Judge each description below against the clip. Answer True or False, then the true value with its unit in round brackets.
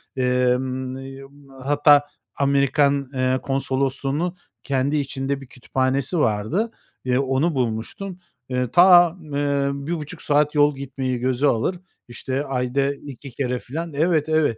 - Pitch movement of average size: False (2.2 semitones)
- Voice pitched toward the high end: False (140 Hz)